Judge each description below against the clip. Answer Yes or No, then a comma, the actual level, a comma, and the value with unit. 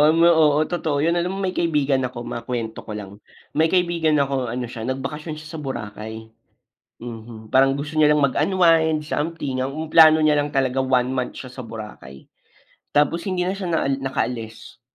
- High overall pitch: No, medium, 140 Hz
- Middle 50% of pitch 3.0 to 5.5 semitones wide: Yes, average, 4.5 semitones